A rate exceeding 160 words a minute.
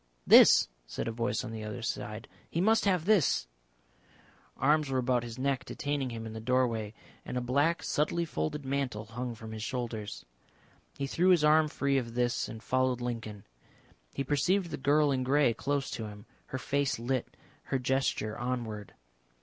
Yes: average, 175 wpm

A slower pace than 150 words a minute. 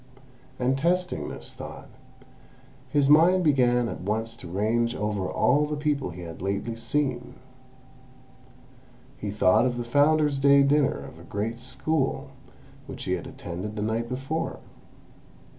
Yes: average, 140 wpm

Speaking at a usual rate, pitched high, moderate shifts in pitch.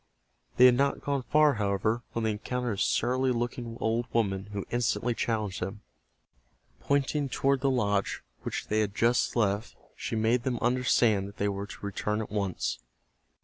No: average, 170 wpm; low, 115 Hz; average, 3.4 semitones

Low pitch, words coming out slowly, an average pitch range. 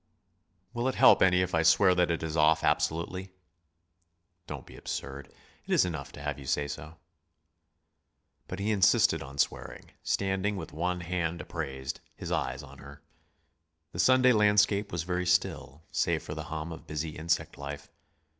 No: very low, 85 Hz; average, 165 wpm; average, 4.0 semitones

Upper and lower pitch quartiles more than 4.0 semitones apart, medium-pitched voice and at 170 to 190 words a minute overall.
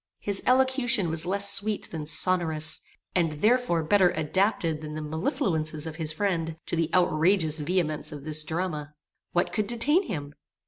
No: average, 4.4 semitones; medium, 165 Hz; average, 155 wpm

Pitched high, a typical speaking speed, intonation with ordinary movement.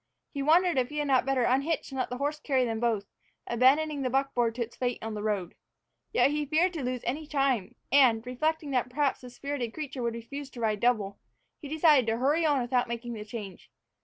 No: very high, 255 Hz; fast, 220 wpm; average, 3.5 semitones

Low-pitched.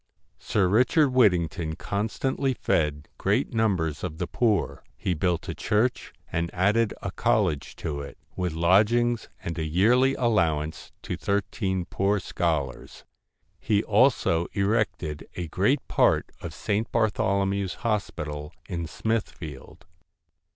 Yes: very low, 95 Hz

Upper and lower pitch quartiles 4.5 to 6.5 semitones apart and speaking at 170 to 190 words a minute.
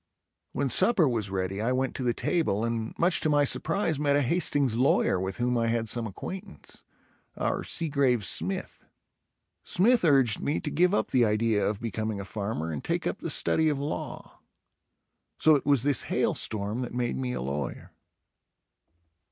Yes: average, 5.1 semitones; average, 175 wpm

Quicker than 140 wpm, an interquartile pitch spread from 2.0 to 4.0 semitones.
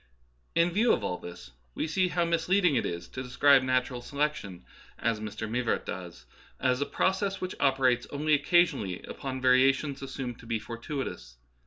No: average, 165 wpm; average, 5.1 semitones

